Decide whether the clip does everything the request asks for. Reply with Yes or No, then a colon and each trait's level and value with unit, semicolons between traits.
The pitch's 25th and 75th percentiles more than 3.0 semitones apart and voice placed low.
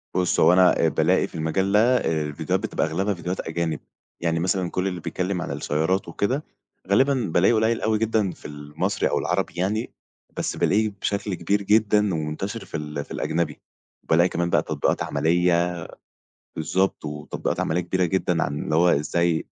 Yes: average, 3.7 semitones; very low, 90 Hz